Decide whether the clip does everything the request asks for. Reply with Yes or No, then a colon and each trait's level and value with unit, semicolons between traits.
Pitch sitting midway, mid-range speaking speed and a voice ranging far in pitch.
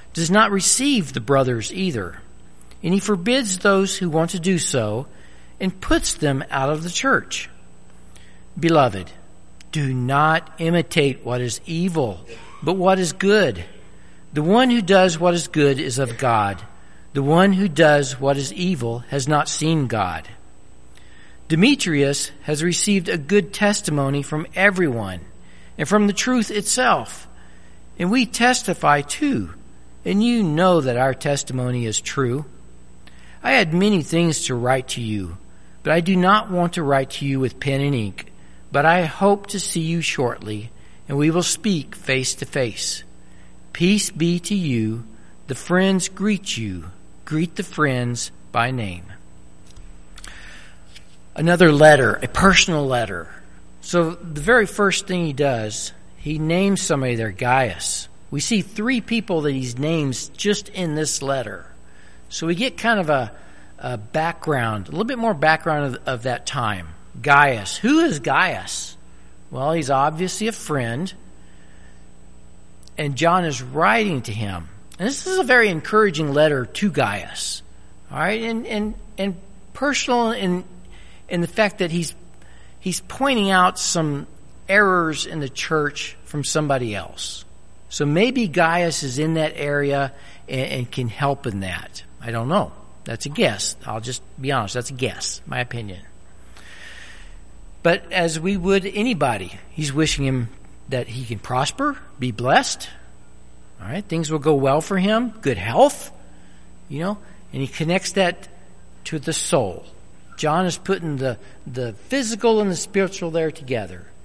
Yes: medium, 150 Hz; average, 150 wpm; wide, 7.9 semitones